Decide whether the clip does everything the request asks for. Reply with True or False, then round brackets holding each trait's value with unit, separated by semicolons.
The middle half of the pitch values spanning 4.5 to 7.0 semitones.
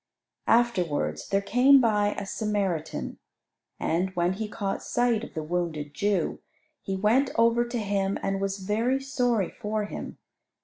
False (3.7 semitones)